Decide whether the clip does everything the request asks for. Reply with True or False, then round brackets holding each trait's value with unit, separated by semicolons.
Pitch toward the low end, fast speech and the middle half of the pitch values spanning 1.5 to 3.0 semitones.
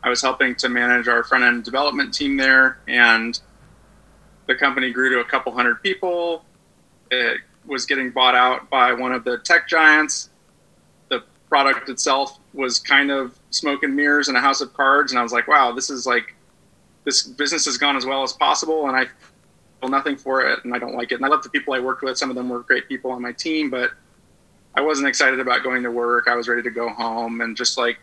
True (130 Hz; 225 wpm; 2.6 semitones)